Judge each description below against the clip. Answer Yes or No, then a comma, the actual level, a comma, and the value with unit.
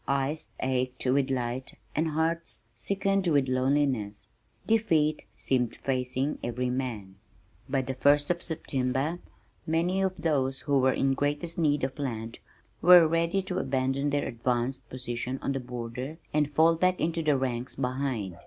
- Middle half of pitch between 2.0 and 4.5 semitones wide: Yes, average, 3.9 semitones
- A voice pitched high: No, low, 135 Hz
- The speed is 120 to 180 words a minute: Yes, average, 150 wpm